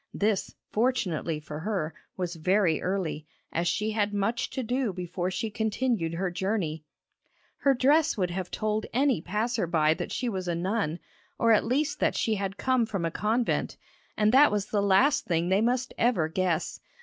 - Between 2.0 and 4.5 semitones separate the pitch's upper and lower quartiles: No, average, 4.9 semitones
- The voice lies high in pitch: Yes, high, 200 Hz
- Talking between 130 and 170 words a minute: No, average, 180 wpm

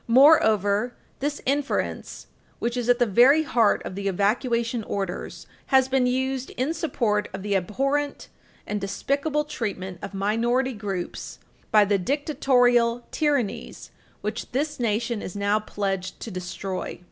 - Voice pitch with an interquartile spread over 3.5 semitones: Yes, average, 4.8 semitones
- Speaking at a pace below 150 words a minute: Yes, slow, 135 wpm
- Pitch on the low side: No, high, 235 Hz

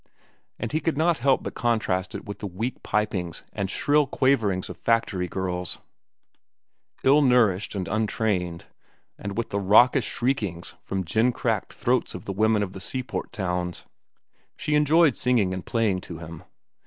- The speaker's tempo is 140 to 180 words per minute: Yes, average, 160 wpm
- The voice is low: Yes, low, 105 Hz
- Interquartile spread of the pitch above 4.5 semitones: Yes, average, 5.2 semitones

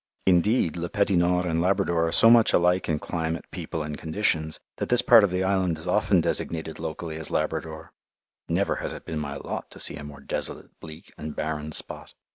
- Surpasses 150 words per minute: Yes, fast, 205 wpm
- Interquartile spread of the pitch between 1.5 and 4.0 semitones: Yes, average, 2.9 semitones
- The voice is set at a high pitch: No, very low, 85 Hz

